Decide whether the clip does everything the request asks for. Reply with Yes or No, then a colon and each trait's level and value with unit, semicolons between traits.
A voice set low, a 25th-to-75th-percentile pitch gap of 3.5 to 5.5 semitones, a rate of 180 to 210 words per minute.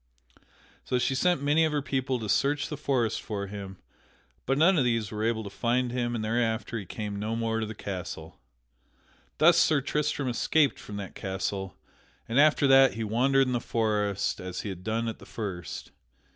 Yes: low, 115 Hz; average, 4.5 semitones; average, 195 wpm